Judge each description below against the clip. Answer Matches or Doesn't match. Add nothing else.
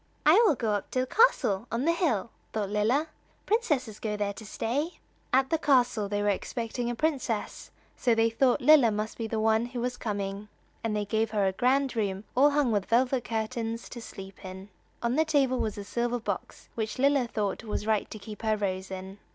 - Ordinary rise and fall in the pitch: Matches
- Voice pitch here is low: Doesn't match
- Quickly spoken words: Matches